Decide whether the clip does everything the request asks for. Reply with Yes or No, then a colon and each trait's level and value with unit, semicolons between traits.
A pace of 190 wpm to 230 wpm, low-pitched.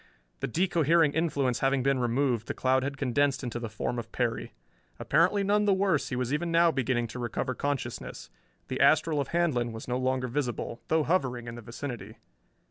Yes: average, 195 wpm; low, 130 Hz